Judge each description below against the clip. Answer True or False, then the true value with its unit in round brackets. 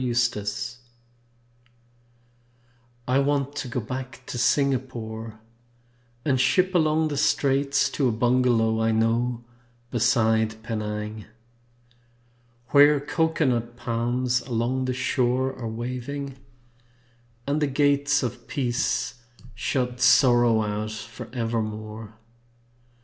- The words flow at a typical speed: False (95 wpm)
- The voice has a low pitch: True (125 Hz)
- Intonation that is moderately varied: True (3.2 semitones)